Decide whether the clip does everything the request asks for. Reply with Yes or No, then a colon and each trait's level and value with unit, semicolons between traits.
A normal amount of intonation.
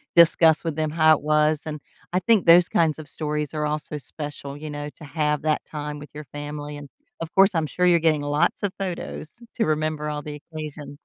No: narrow, 1.6 semitones